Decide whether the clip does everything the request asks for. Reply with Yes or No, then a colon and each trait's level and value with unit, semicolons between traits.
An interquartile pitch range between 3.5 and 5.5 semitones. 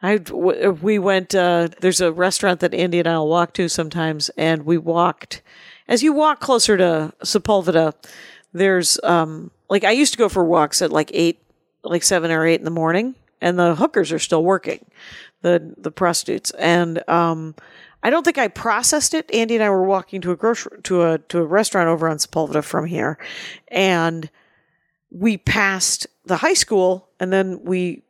No: average, 3.0 semitones